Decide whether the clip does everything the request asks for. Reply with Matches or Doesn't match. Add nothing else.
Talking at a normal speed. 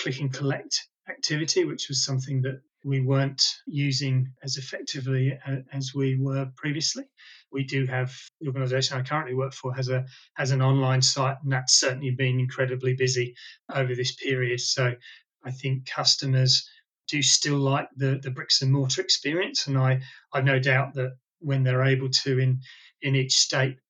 Matches